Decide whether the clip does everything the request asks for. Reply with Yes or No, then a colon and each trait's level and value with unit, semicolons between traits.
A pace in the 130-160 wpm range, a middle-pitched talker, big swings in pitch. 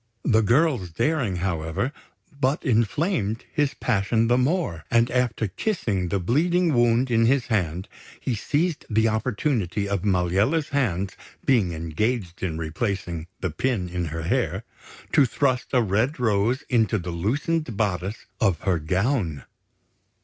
No: average, 140 wpm; low, 110 Hz; wide, 6.0 semitones